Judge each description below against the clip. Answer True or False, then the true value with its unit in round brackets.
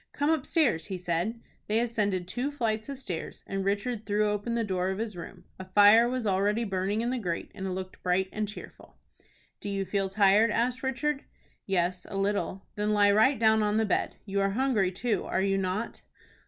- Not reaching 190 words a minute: False (205 wpm)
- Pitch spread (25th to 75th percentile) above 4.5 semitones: False (3.2 semitones)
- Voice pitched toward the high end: True (205 Hz)